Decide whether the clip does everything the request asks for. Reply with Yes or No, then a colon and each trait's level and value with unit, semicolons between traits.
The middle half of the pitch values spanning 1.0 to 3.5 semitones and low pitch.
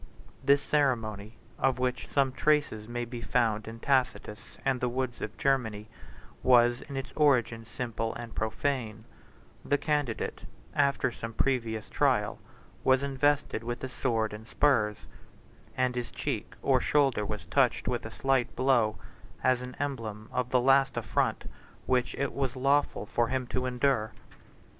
Yes: average, 3.1 semitones; low, 125 Hz